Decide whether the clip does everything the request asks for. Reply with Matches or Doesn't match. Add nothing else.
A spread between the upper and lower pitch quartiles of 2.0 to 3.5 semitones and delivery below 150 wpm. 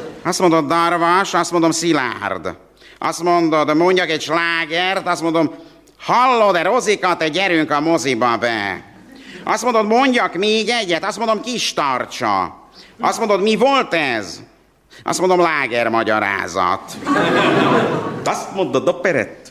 Doesn't match